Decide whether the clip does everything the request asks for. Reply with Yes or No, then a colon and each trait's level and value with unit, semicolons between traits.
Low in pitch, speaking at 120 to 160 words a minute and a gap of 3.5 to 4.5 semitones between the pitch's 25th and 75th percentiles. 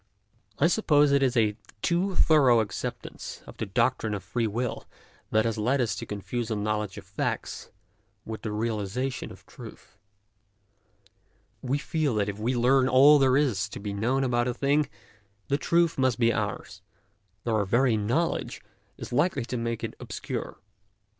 No: low, 120 Hz; average, 170 wpm; average, 4.1 semitones